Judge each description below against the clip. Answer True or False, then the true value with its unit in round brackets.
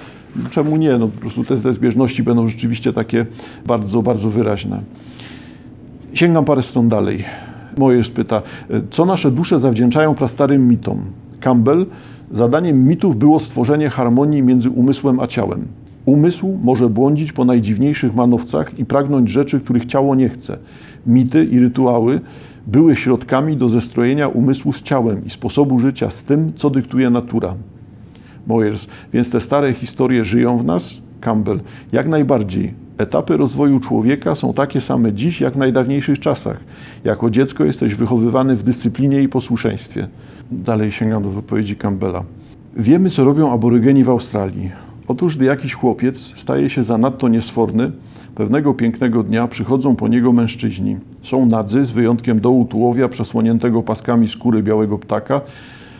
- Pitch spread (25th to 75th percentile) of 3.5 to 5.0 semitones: False (2.9 semitones)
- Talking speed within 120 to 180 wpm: True (145 wpm)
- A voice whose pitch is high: False (125 Hz)